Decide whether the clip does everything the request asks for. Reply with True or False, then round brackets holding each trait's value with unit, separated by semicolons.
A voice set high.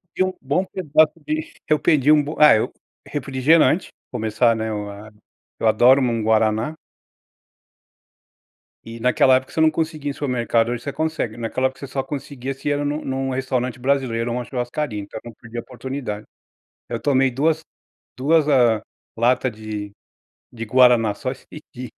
False (130 Hz)